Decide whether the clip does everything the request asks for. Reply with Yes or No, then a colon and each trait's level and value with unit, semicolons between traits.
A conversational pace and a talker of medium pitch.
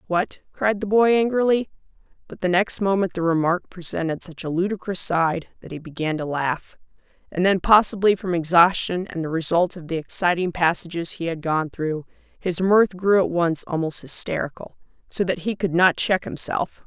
Yes: average, 180 wpm; medium, 180 Hz